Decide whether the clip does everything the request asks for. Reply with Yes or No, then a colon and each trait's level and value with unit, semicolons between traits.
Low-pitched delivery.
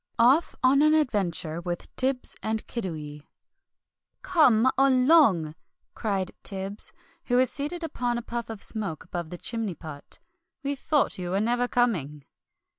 No: high, 225 Hz